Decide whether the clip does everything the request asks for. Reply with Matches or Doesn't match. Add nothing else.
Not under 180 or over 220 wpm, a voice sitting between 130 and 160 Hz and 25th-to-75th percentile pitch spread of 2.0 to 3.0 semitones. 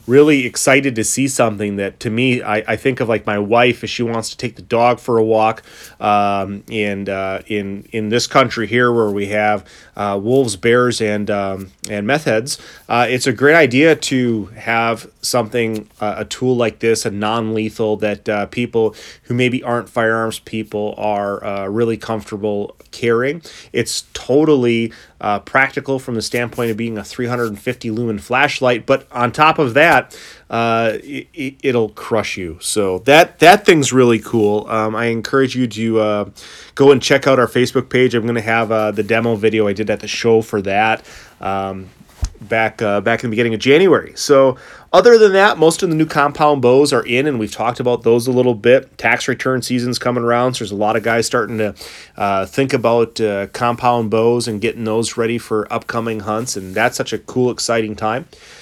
Doesn't match